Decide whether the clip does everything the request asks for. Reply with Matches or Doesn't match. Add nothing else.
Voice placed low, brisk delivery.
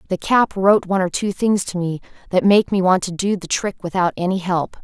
Doesn't match